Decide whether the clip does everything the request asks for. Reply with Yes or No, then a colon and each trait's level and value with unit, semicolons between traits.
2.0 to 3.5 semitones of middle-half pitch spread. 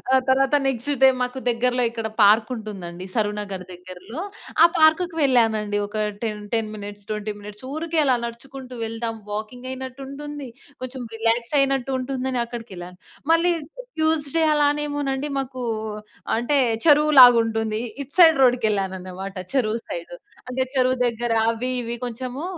No: average, 4.0 semitones